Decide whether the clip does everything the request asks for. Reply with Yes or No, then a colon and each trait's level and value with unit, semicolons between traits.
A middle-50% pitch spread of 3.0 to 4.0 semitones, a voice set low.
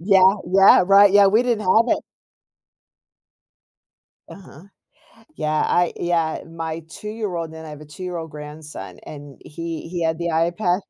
No: average, 3.4 semitones; medium, 170 Hz